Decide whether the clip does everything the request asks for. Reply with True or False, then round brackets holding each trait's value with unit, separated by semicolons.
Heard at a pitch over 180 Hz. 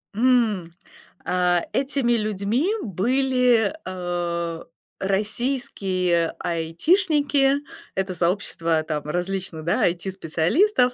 True (190 Hz)